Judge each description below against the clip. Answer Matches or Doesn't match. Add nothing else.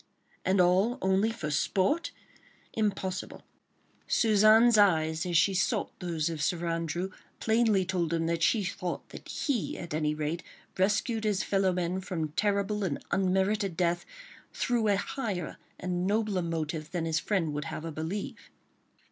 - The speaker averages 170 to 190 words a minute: Doesn't match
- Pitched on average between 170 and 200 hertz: Matches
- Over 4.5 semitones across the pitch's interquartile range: Doesn't match